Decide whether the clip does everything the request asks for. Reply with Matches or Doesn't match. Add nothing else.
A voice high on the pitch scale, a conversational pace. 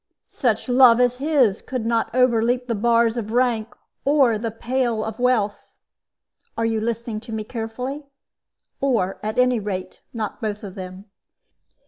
Matches